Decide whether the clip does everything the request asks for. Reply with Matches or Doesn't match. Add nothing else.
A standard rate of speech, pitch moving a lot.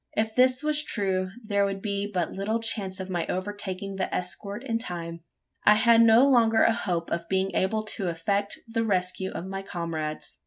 Doesn't match